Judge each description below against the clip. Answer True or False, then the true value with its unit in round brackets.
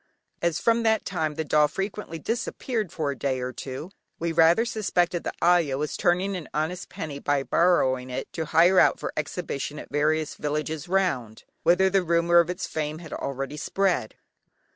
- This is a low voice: False (165 Hz)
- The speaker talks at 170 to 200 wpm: True (180 wpm)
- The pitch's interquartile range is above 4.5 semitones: False (3.5 semitones)